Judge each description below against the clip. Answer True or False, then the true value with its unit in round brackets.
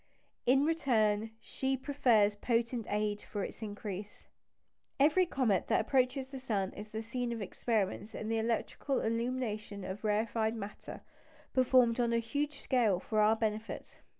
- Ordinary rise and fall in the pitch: True (3.3 semitones)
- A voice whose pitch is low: False (225 Hz)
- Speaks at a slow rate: False (150 wpm)